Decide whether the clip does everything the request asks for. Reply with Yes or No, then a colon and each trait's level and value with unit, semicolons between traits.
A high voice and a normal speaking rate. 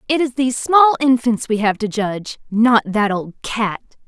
Yes: high, 235 Hz; average, 190 wpm